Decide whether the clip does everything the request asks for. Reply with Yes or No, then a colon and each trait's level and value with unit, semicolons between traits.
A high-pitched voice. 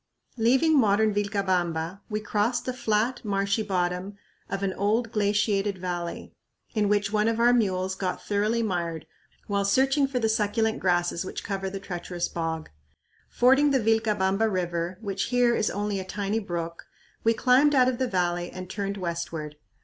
Yes: high, 205 Hz